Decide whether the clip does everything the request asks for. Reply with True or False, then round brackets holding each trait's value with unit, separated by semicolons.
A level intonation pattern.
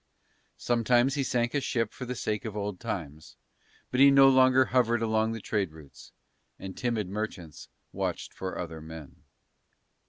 False (5.3 semitones)